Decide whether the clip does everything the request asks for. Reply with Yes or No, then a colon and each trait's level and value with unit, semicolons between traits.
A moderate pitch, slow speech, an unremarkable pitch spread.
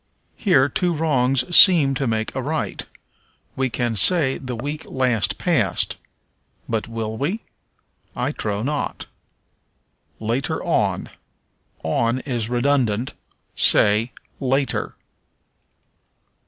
No: low, 130 Hz; slow, 100 wpm; average, 3.8 semitones